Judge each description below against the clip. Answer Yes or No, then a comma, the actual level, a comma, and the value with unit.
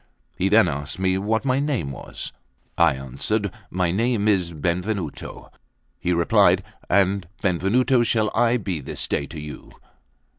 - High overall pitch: No, very low, 95 Hz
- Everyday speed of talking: Yes, average, 145 wpm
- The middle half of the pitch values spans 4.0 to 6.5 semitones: Yes, average, 4.5 semitones